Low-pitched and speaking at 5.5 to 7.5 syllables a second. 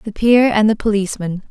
No: high, 210 Hz; 5.9 syllables/s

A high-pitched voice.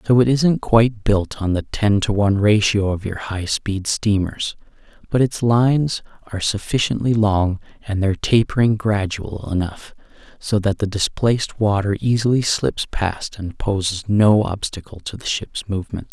No: low, 105 Hz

